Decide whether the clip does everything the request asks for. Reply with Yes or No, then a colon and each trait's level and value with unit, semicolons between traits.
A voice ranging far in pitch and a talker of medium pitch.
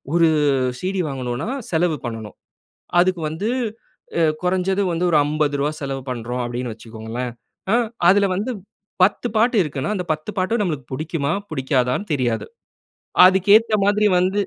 Yes: wide, 6.7 semitones; medium, 155 Hz